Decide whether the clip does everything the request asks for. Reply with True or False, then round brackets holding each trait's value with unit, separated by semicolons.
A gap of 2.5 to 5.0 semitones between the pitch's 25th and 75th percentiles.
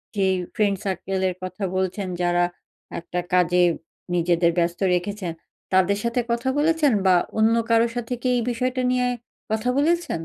False (5.4 semitones)